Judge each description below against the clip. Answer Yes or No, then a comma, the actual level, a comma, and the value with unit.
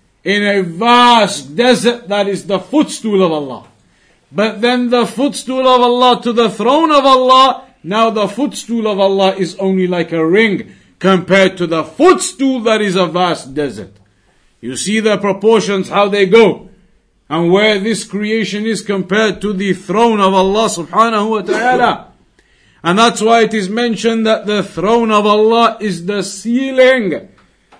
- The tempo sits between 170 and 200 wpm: No, average, 160 wpm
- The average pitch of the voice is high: Yes, high, 210 Hz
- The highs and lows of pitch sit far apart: No, average, 3.5 semitones